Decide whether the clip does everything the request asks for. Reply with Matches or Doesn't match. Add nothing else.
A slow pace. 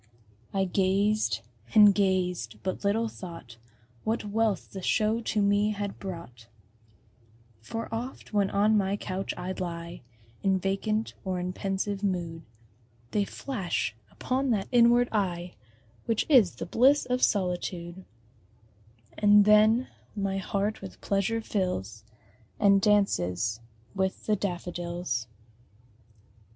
Matches